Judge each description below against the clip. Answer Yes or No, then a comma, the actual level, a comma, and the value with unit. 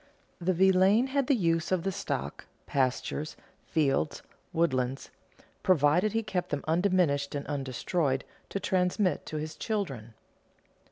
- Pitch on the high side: No, medium, 165 Hz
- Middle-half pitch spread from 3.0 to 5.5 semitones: Yes, average, 5.1 semitones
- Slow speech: Yes, slow, 125 wpm